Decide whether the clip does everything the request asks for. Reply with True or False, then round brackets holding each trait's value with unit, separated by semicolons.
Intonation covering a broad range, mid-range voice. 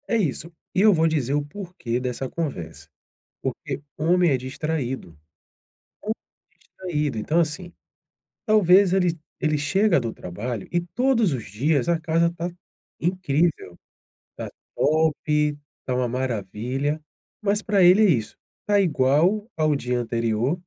True (5.8 semitones; 155 Hz)